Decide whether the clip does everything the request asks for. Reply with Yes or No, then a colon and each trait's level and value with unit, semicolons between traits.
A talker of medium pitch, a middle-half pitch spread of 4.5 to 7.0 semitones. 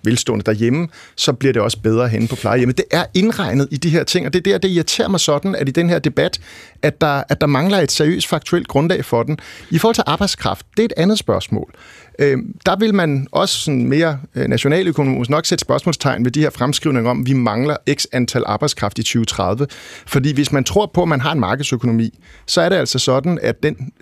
Yes: medium, 145 Hz; wide, 5.6 semitones